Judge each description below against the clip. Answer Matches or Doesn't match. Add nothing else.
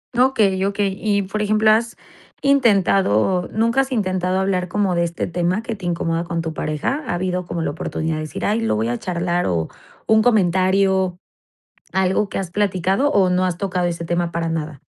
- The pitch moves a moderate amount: Matches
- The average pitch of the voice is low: Doesn't match